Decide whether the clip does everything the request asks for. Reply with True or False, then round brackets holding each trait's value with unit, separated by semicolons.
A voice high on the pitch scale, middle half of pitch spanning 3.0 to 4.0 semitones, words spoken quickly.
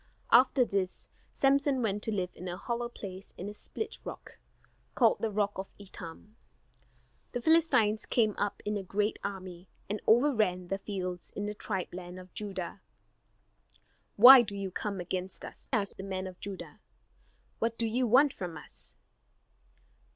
False (205 Hz; 3.7 semitones; 160 wpm)